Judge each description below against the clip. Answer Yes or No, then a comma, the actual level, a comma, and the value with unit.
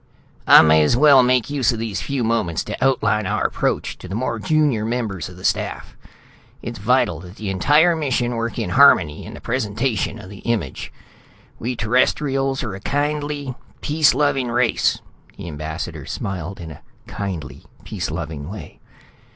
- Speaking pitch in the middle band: No, low, 115 Hz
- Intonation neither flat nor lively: No, wide, 5.9 semitones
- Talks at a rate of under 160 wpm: No, average, 165 wpm